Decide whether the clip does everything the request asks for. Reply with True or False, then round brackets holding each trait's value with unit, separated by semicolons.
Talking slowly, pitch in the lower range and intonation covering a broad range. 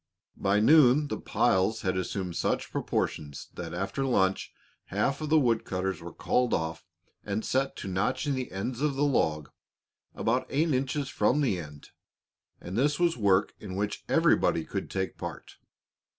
False (165 wpm; 110 Hz; 6.4 semitones)